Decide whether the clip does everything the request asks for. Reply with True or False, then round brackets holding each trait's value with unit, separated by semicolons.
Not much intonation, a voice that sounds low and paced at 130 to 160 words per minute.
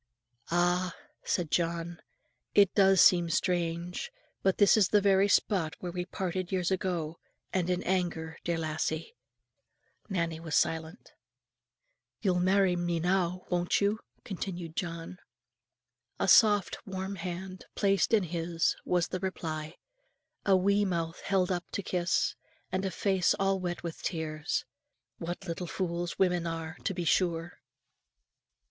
False (2.2 semitones; 180 Hz; 140 wpm)